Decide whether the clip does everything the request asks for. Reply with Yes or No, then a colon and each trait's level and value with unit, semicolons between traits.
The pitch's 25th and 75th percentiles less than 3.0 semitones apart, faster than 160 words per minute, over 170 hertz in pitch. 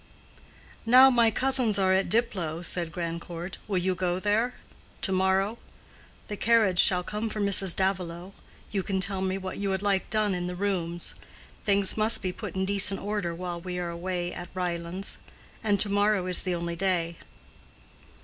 Yes: narrow, 2.5 semitones; average, 170 wpm; high, 190 Hz